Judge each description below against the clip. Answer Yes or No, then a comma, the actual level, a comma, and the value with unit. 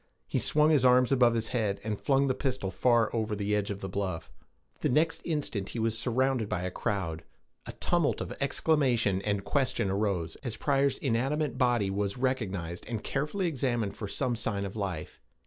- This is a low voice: Yes, low, 115 Hz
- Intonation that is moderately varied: Yes, average, 4.8 semitones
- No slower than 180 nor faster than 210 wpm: Yes, average, 185 wpm